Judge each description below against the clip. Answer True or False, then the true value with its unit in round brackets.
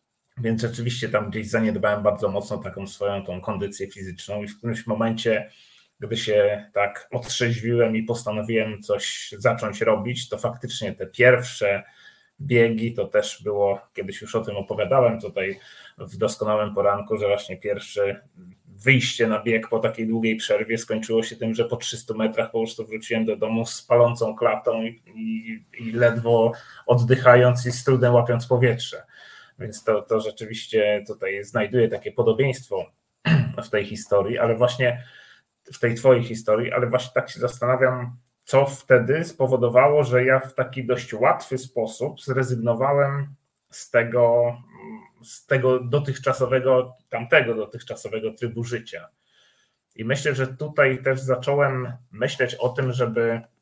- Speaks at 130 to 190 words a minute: True (145 wpm)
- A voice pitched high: False (120 Hz)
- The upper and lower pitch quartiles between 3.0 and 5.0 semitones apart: False (2.6 semitones)